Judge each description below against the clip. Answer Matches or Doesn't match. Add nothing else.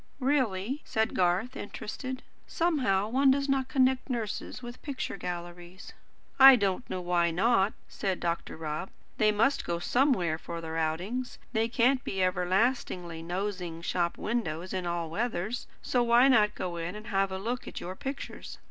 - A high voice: Matches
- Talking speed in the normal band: Matches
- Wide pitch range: Matches